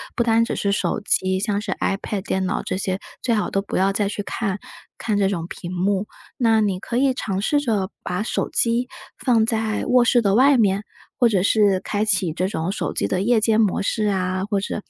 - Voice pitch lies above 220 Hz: No, high, 205 Hz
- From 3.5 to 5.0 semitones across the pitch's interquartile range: No, average, 2.8 semitones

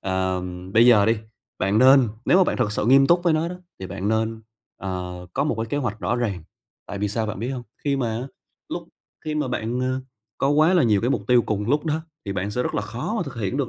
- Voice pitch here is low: Yes, low, 120 Hz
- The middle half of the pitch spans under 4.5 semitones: No, average, 4.9 semitones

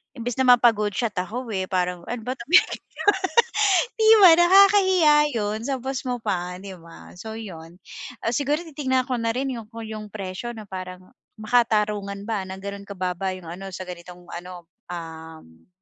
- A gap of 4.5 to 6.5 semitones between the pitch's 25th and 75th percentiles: Yes, average, 5.2 semitones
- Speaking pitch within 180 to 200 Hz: No, high, 210 Hz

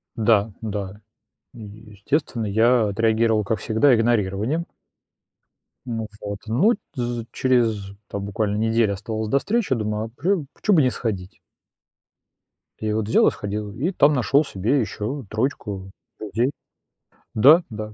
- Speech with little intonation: No, average, 3.5 semitones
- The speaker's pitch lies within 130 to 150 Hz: No, low, 110 Hz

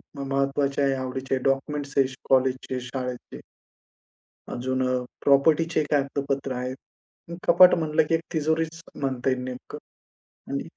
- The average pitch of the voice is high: No, low, 135 Hz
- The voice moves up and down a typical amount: No, narrow, 2.2 semitones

